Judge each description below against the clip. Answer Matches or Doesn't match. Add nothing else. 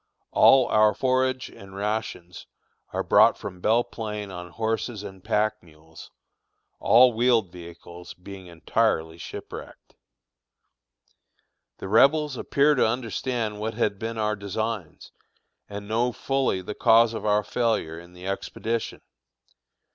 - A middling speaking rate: Doesn't match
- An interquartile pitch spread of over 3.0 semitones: Matches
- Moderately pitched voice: Doesn't match